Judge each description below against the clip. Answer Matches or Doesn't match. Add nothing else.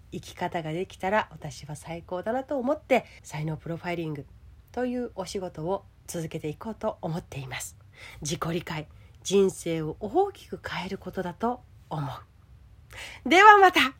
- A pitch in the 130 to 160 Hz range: Doesn't match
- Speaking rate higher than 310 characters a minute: Doesn't match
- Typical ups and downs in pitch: Doesn't match